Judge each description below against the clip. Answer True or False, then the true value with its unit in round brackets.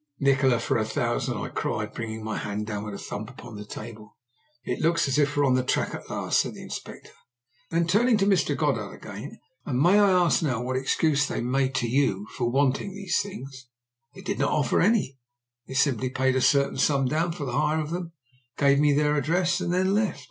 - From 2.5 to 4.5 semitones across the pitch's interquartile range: False (5.1 semitones)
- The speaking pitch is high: False (140 Hz)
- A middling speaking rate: False (220 wpm)